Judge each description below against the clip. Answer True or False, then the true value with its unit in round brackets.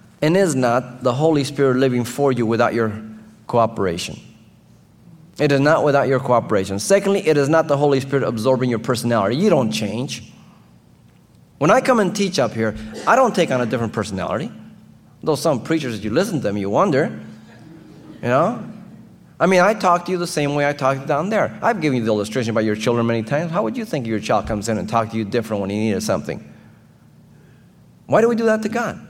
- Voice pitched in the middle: False (125 Hz)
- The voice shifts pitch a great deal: True (5.9 semitones)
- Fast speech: True (215 wpm)